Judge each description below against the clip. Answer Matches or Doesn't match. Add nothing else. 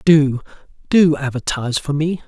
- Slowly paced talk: Matches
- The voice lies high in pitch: Doesn't match